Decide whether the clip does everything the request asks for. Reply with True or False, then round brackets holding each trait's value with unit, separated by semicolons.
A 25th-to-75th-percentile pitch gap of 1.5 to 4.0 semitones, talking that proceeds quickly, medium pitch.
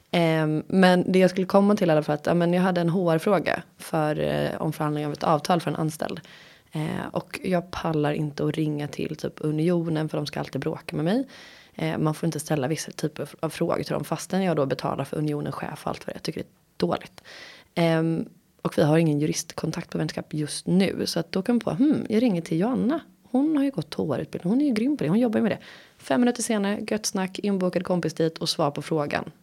True (3.7 semitones; 230 wpm; 170 Hz)